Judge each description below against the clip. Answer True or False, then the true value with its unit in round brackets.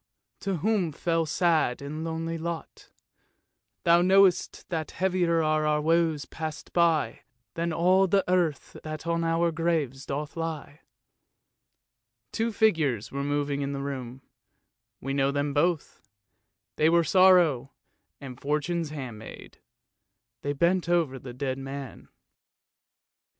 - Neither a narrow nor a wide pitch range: True (3.3 semitones)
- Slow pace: True (130 wpm)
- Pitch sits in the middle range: True (160 Hz)